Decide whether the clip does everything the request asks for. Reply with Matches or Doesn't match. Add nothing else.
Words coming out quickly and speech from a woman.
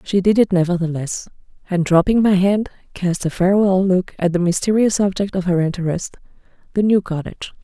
Doesn't match